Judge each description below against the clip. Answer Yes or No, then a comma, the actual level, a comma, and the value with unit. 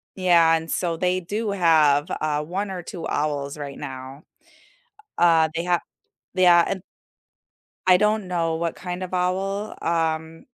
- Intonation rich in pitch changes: No, narrow, 2.5 semitones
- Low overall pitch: No, medium, 170 Hz